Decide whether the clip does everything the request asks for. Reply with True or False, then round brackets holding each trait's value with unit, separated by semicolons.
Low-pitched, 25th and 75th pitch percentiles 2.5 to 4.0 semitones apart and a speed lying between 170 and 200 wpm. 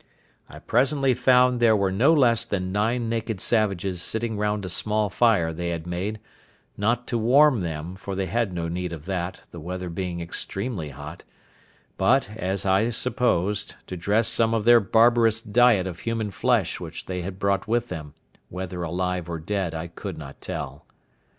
False (100 Hz; 4.6 semitones; 175 wpm)